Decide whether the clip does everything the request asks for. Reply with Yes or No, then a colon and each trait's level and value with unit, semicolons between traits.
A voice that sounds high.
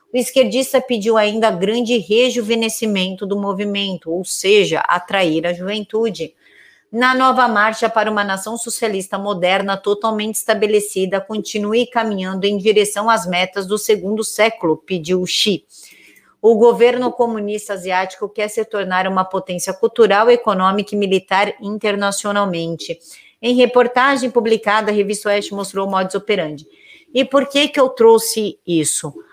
Yes: high, 210 Hz